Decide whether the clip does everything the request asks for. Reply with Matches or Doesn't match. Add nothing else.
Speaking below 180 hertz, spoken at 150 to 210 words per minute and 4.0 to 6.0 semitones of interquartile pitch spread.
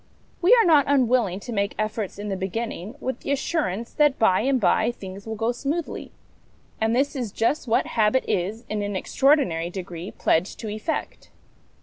Doesn't match